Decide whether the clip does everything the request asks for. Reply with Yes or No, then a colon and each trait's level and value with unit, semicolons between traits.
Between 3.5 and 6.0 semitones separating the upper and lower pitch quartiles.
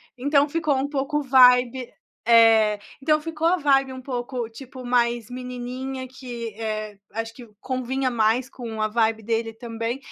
No: average, 2.8 semitones